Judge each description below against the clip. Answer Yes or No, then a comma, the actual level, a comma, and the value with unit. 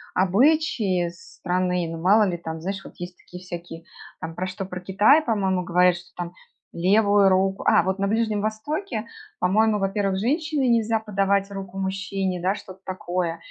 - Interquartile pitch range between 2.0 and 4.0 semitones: Yes, average, 2.9 semitones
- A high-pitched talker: Yes, high, 195 Hz